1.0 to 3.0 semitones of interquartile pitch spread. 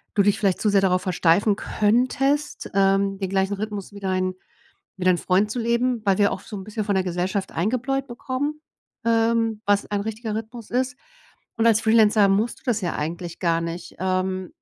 No: average, 3.4 semitones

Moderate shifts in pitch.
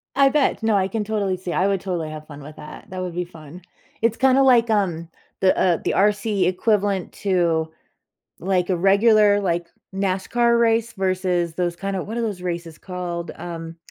Yes: average, 3.4 semitones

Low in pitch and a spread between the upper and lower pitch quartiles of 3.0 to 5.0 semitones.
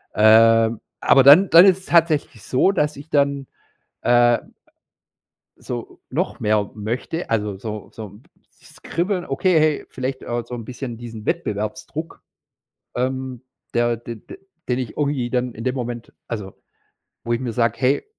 Yes: low, 125 Hz; average, 3.8 semitones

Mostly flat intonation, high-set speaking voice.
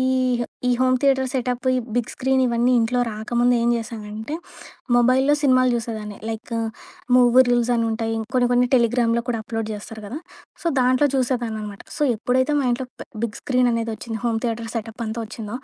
Yes: narrow, 2.2 semitones; high, 240 Hz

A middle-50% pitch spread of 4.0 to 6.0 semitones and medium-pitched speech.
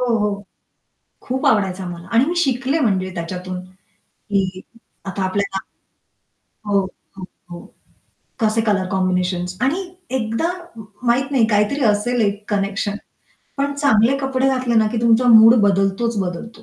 No: average, 4.4 semitones; high, 215 Hz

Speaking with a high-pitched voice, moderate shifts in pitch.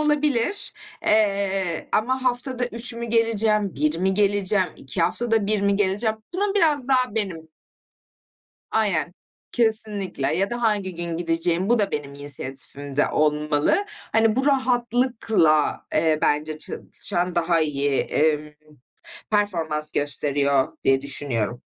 No: high, 195 Hz; wide, 6.9 semitones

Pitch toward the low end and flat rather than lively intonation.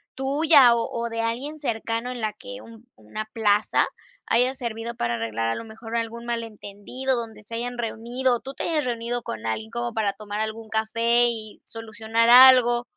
No: high, 230 Hz; narrow, 1.8 semitones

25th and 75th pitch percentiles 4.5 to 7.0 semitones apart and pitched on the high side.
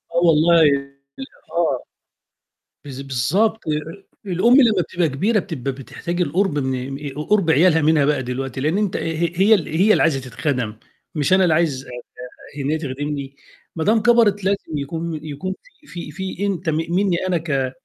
No: average, 4.9 semitones; medium, 160 Hz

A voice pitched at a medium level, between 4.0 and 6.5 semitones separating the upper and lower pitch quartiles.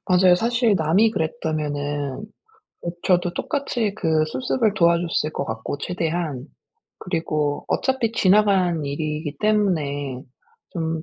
Yes: medium, 170 Hz; average, 5.2 semitones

